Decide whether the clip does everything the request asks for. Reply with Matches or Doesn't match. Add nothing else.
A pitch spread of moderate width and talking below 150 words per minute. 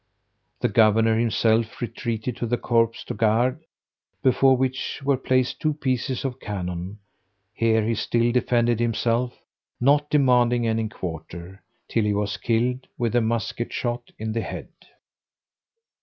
Doesn't match